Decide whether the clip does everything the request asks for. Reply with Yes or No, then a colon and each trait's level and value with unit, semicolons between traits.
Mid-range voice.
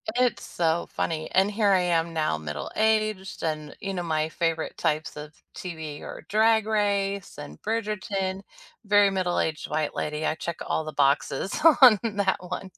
Yes: medium, 180 Hz